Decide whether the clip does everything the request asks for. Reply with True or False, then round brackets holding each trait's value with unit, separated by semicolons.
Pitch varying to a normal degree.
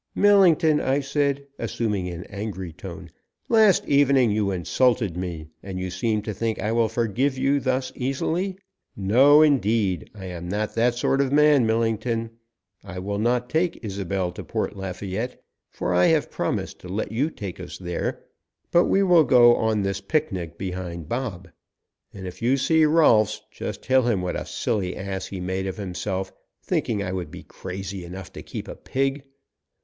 False (6.1 semitones)